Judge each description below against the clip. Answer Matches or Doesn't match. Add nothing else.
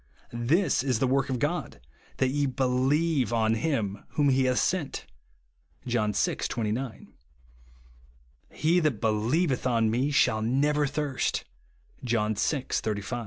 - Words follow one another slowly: Doesn't match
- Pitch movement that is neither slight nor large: Matches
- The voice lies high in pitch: Doesn't match